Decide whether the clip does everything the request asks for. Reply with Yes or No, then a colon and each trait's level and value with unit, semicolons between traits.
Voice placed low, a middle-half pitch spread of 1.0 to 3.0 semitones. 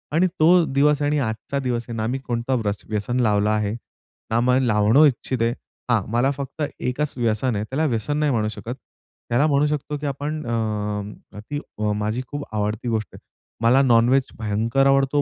No: low, 125 Hz; average, 4.0 semitones